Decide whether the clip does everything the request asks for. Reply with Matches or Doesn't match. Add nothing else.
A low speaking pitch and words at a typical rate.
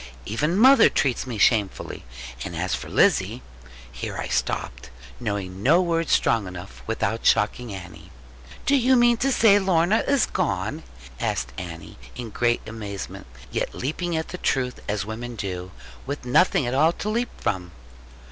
Matches